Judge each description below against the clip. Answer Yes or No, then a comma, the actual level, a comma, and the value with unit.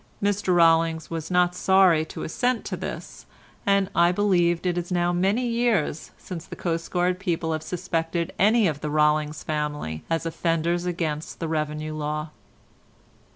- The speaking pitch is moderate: Yes, medium, 170 Hz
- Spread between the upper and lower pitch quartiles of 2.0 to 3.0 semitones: Yes, narrow, 2.6 semitones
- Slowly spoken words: No, average, 155 wpm